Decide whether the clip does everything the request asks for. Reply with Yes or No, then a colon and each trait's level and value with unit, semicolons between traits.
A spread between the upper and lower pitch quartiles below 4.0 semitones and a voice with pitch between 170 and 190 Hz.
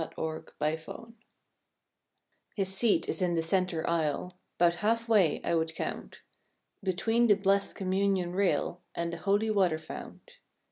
Yes: average, 3.2 semitones; medium, 185 Hz